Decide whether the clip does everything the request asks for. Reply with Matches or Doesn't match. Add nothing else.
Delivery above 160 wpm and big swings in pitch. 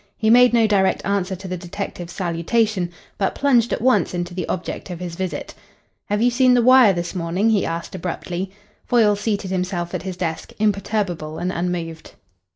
Doesn't match